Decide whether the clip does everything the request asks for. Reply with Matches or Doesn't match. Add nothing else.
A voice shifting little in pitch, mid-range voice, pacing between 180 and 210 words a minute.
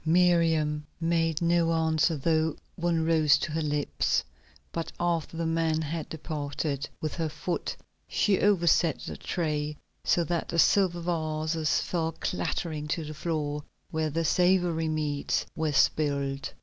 Doesn't match